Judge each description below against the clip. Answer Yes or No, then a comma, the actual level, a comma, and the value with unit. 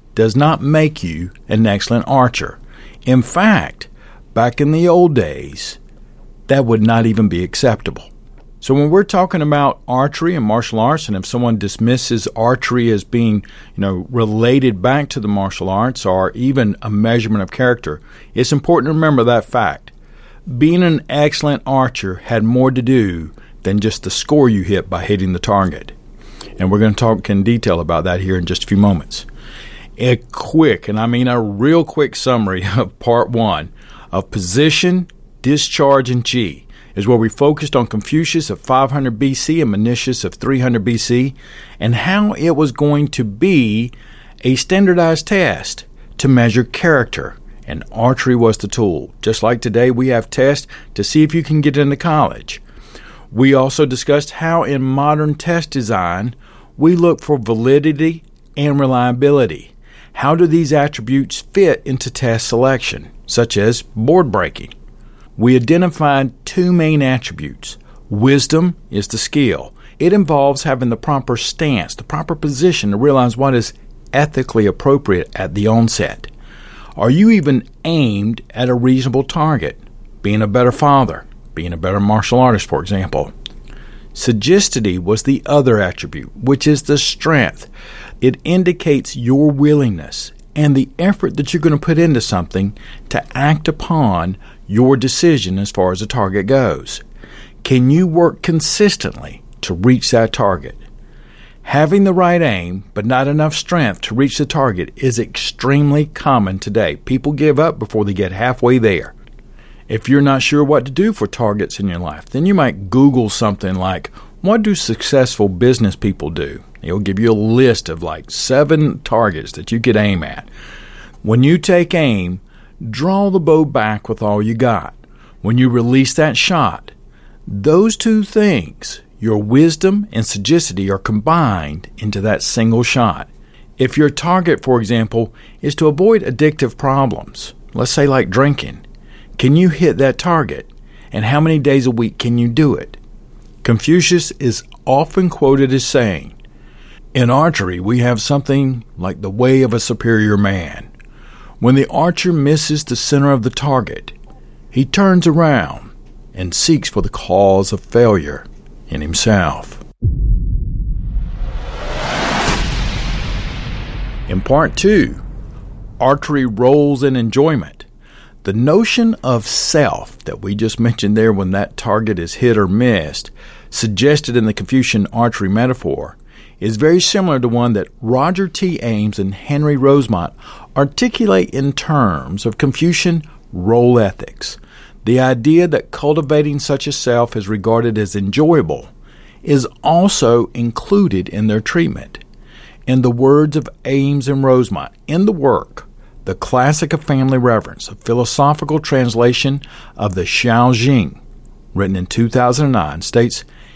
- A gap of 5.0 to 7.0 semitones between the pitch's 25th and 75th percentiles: Yes, average, 5.3 semitones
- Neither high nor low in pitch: No, low, 125 Hz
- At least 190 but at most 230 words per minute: No, average, 150 wpm